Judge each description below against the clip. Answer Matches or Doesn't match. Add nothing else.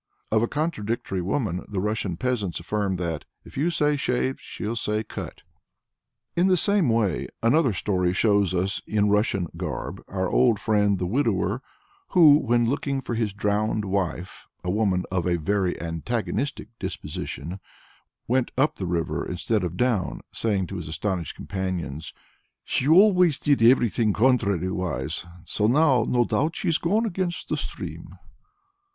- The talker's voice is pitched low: Matches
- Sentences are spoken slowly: Doesn't match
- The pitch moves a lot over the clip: Matches